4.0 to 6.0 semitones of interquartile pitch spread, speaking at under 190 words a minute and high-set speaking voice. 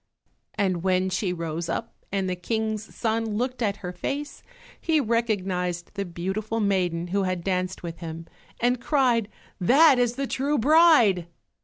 Yes: average, 4.8 semitones; average, 155 wpm; high, 200 Hz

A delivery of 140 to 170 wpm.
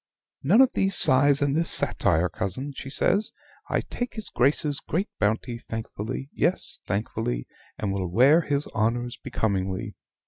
Yes: average, 145 wpm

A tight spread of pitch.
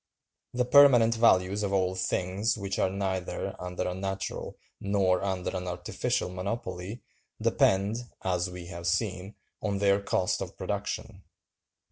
Yes: narrow, 1.9 semitones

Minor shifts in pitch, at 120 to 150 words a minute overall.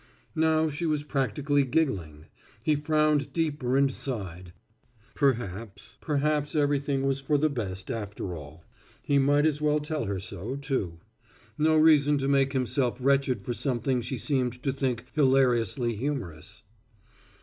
No: average, 3.9 semitones; average, 140 wpm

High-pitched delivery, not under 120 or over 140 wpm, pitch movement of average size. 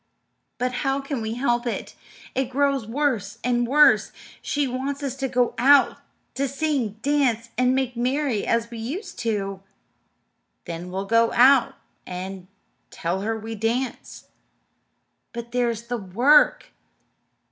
Yes: high, 245 Hz; slow, 135 wpm; average, 3.3 semitones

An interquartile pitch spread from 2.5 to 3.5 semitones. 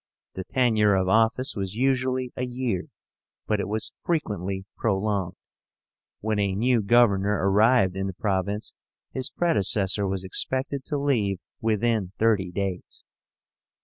No: average, 4.1 semitones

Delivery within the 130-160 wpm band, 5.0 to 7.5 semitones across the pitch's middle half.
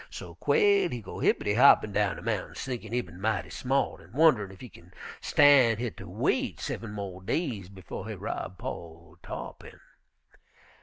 No: average, 175 wpm; average, 5.3 semitones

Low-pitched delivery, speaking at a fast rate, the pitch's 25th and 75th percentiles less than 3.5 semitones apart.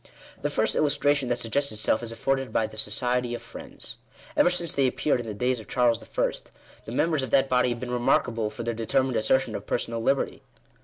Yes: low, 125 Hz; fast, 210 wpm; average, 2.8 semitones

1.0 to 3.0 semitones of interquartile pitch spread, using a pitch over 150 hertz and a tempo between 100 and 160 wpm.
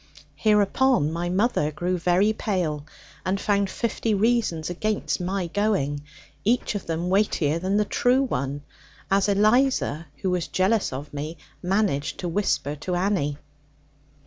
No: average, 4.5 semitones; medium, 185 Hz; average, 140 wpm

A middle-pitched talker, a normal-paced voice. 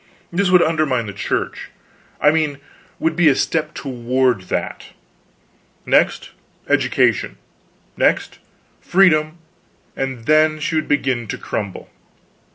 No: medium, 150 Hz; slow, 115 wpm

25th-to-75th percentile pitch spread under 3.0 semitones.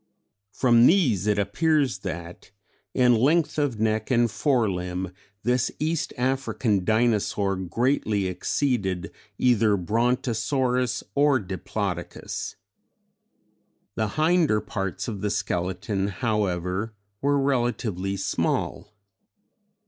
No: average, 4.8 semitones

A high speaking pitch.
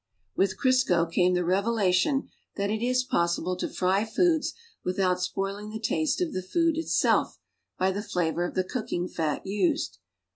Yes: high, 195 Hz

